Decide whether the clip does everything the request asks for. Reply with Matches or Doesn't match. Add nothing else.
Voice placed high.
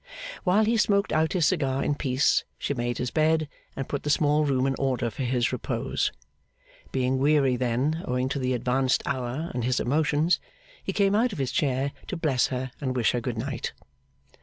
Doesn't match